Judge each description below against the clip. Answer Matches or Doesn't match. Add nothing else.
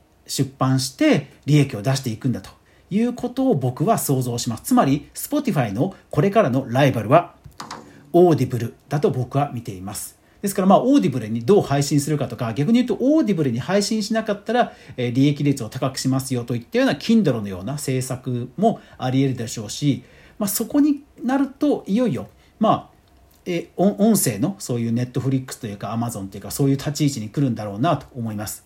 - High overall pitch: Doesn't match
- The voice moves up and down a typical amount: Doesn't match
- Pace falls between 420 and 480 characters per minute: Matches